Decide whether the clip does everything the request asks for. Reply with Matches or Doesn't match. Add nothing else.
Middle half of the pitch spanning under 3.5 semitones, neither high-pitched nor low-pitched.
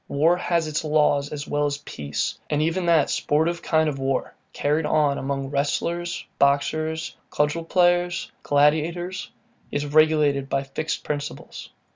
Matches